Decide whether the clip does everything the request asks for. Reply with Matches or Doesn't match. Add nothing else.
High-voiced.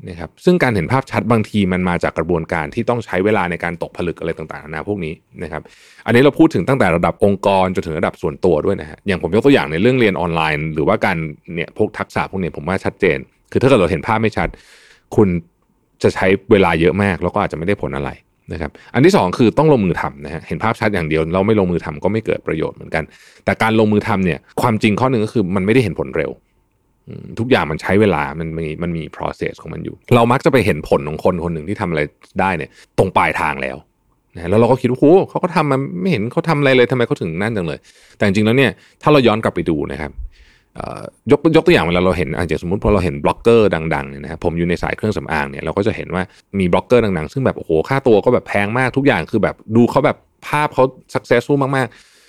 Doesn't match